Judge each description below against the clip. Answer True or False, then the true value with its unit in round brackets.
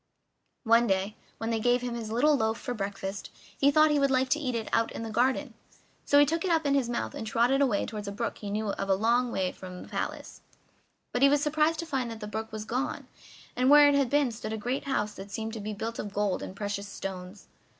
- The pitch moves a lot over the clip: False (4.6 semitones)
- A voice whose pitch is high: True (230 Hz)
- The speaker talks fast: True (260 wpm)